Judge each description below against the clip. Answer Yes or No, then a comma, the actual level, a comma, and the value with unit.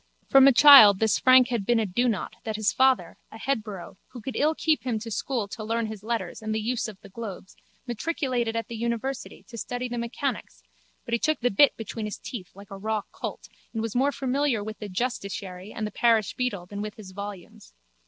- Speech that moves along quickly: Yes, fast, 220 wpm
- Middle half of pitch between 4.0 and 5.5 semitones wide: No, average, 3.3 semitones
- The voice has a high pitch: Yes, high, 225 Hz